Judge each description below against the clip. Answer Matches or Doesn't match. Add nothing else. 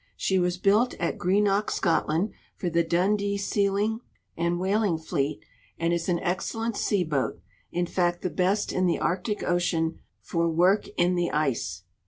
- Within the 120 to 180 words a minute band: Matches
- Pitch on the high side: Doesn't match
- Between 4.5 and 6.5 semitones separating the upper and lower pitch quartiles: Doesn't match